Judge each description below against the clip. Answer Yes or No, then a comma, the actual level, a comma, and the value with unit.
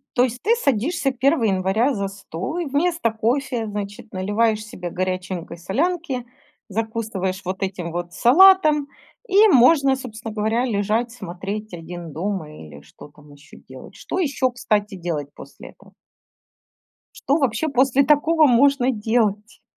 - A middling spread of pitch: No, wide, 6.2 semitones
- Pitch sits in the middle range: No, high, 220 Hz